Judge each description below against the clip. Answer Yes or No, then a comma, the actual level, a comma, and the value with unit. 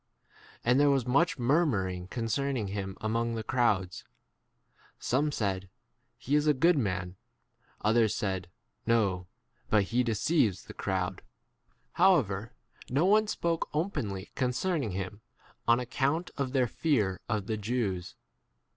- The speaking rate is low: Yes, slow, 130 wpm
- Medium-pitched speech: No, low, 115 Hz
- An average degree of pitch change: No, wide, 6.1 semitones